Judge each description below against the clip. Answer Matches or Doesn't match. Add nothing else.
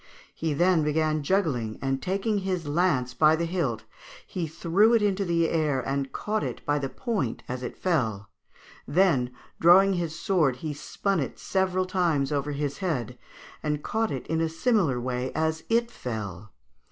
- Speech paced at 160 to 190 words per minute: Matches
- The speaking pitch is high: Doesn't match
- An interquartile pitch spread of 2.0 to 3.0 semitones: Doesn't match